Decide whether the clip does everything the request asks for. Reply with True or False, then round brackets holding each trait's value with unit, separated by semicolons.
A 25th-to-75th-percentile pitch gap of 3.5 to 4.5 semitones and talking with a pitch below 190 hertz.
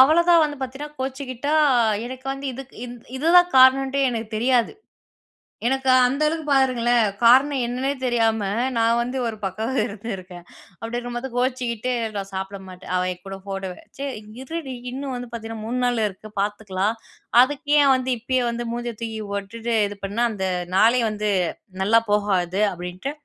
False (3.8 semitones; 240 Hz)